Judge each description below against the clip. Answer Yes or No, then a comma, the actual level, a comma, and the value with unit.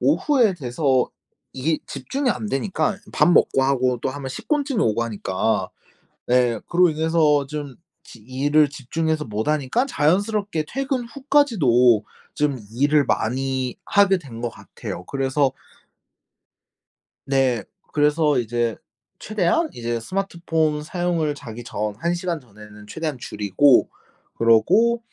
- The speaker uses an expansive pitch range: Yes, wide, 6.1 semitones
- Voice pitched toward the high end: No, medium, 145 Hz